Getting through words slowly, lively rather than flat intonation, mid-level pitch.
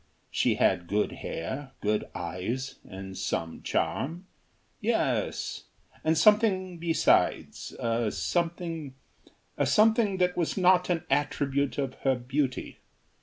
Yes: slow, 115 wpm; wide, 6.8 semitones; medium, 145 Hz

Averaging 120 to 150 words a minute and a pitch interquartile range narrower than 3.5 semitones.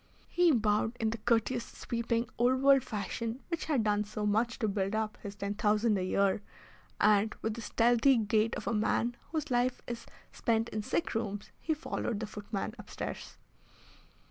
No: average, 175 wpm; narrow, 2.4 semitones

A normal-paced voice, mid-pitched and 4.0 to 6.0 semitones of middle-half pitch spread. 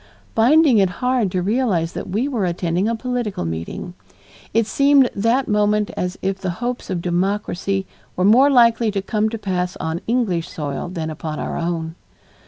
No: average, 175 wpm; high, 200 Hz; average, 4.8 semitones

